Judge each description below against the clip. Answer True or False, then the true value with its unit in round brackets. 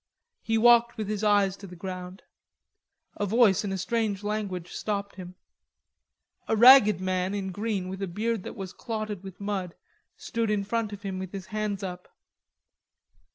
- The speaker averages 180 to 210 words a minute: False (170 wpm)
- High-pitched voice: True (200 Hz)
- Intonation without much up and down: True (2.3 semitones)